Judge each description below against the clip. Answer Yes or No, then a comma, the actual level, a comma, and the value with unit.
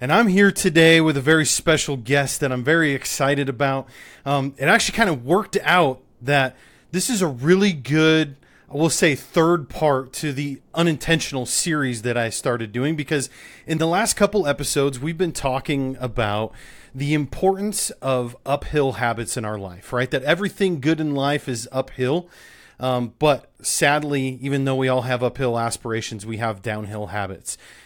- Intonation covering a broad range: No, average, 4.2 semitones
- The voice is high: No, medium, 140 Hz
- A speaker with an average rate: Yes, average, 170 wpm